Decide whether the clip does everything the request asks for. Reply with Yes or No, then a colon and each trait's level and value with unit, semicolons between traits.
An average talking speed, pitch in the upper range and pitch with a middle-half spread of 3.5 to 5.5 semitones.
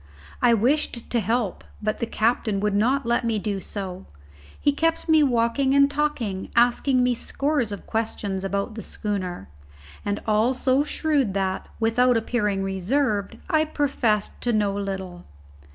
Yes: average, 150 wpm; high, 225 Hz; average, 4.6 semitones